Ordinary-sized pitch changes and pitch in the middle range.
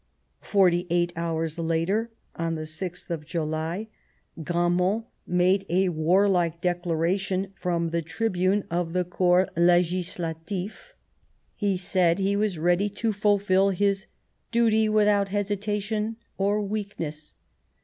Yes: average, 3.0 semitones; medium, 180 Hz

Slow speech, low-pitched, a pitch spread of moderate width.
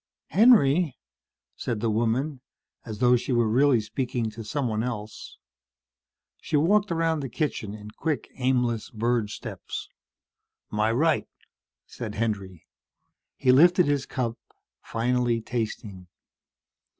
Yes: slow, 115 wpm; low, 120 Hz; average, 4.4 semitones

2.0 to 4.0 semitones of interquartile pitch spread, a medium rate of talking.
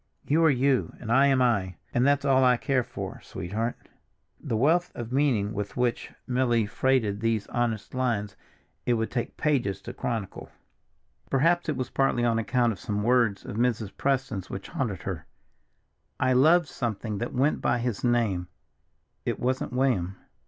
Yes: average, 3.7 semitones; average, 165 wpm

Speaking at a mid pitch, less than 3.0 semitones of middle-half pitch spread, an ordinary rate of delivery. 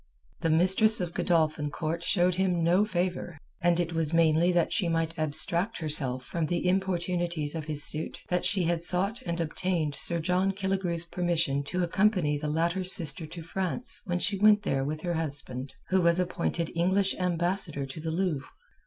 Yes: medium, 170 Hz; narrow, 2.5 semitones; average, 180 wpm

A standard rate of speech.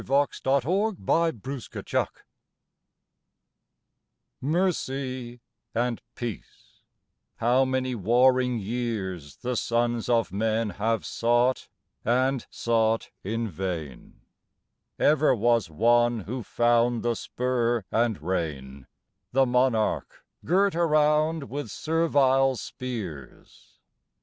No: slow, 100 wpm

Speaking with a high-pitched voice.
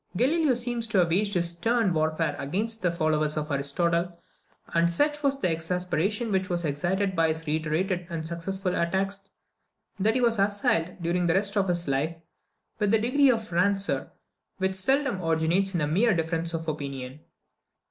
No: medium, 180 Hz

